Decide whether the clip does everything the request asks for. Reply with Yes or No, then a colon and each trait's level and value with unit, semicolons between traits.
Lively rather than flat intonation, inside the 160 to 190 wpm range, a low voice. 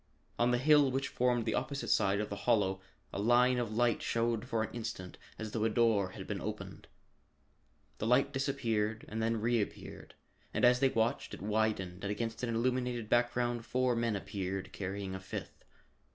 No: average, 2.8 semitones; average, 180 wpm; low, 115 Hz